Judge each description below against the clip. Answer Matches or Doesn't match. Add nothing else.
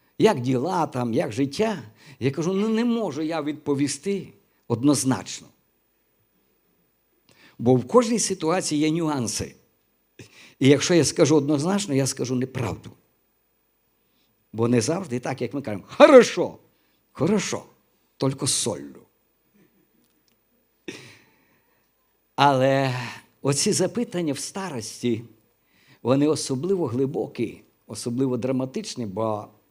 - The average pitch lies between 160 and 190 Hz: Doesn't match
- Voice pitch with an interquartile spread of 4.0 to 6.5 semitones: Matches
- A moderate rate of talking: Doesn't match